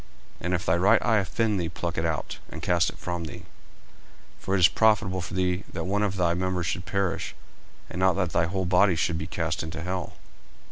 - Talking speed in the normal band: No, fast, 225 wpm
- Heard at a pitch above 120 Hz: No, very low, 90 Hz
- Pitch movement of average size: No, narrow, 2.0 semitones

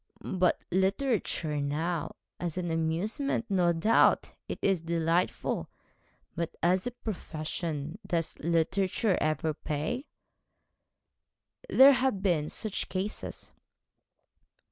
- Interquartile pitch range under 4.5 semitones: Yes, average, 3.7 semitones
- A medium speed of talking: No, slow, 100 wpm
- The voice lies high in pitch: No, medium, 175 Hz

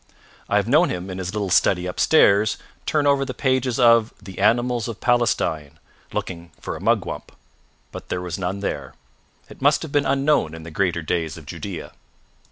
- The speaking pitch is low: Yes, low, 100 Hz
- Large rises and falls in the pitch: Yes, wide, 6.0 semitones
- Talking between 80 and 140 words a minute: No, average, 180 wpm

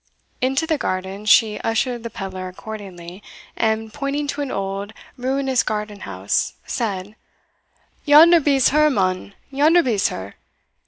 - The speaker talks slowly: Yes, slow, 130 wpm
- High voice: Yes, high, 220 Hz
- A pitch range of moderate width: No, wide, 6.2 semitones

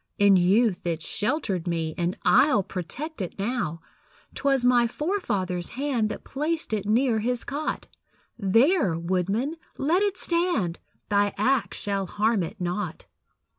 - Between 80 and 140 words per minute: Yes, slow, 135 wpm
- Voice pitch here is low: No, high, 215 Hz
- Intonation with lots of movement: Yes, wide, 6.8 semitones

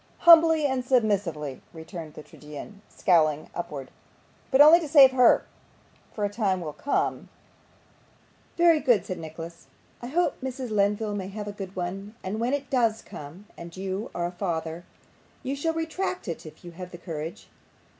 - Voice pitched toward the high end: Yes, high, 200 Hz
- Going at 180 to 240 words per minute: No, average, 170 wpm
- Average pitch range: No, wide, 7.4 semitones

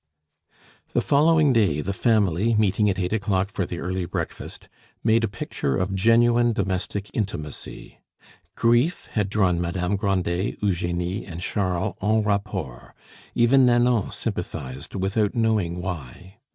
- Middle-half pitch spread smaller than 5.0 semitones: Yes, average, 3.9 semitones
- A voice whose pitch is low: Yes, low, 100 Hz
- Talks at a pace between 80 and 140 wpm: Yes, slow, 135 wpm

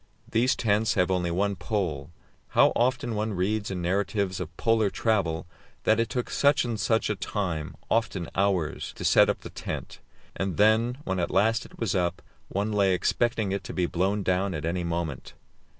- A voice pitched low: Yes, low, 100 Hz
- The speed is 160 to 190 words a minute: Yes, average, 185 wpm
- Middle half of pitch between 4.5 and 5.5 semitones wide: No, average, 3.7 semitones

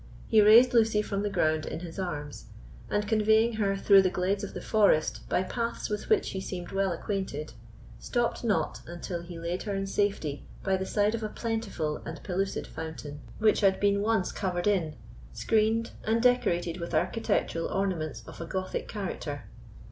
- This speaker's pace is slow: No, average, 180 wpm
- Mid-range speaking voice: No, high, 195 Hz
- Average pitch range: Yes, average, 3.8 semitones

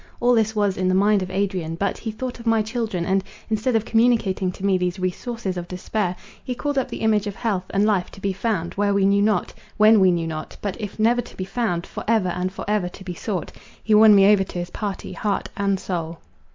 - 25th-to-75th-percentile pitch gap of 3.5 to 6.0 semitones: No, average, 3.0 semitones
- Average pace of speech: No, fast, 245 wpm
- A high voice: Yes, high, 200 Hz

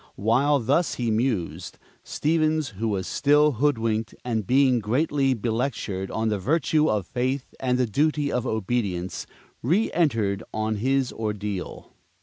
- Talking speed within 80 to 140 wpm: Yes, slow, 135 wpm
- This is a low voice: Yes, low, 120 Hz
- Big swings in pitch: No, average, 4.6 semitones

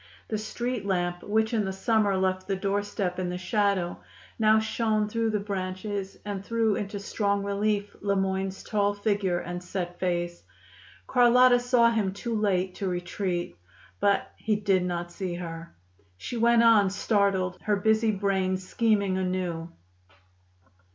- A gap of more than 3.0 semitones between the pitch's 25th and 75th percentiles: No, narrow, 2.6 semitones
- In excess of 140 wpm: Yes, average, 150 wpm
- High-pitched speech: Yes, high, 200 Hz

